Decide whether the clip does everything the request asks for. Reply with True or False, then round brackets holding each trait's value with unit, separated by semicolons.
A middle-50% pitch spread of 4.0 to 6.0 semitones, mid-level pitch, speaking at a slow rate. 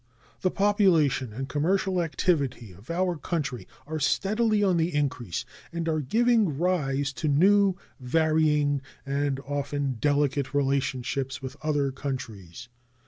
True (4.3 semitones; 145 Hz; 125 wpm)